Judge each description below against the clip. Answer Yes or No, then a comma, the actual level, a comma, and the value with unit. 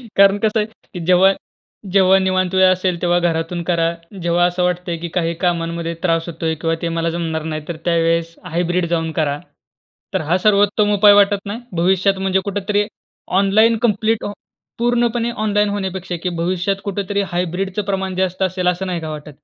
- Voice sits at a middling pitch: Yes, medium, 180 Hz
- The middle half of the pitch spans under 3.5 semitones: Yes, average, 2.9 semitones